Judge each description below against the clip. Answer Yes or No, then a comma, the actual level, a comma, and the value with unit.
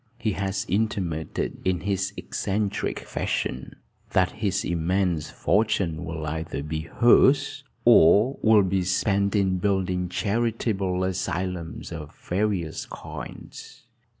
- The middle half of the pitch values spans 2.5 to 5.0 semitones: Yes, average, 3.0 semitones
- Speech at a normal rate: No, slow, 110 wpm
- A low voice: Yes, very low, 95 Hz